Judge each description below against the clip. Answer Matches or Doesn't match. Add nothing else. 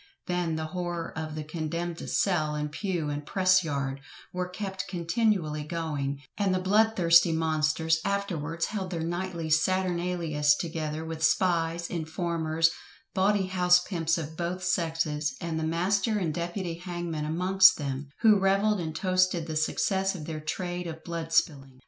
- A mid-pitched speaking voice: Matches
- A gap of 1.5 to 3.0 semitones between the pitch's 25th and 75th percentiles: Matches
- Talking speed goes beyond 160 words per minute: Doesn't match